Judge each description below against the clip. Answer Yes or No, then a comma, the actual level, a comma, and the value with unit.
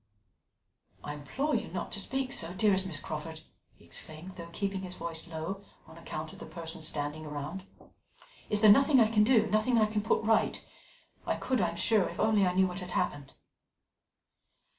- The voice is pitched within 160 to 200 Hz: Yes, medium, 185 Hz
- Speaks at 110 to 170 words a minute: No, average, 190 wpm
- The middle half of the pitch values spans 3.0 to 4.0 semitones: No, average, 5.0 semitones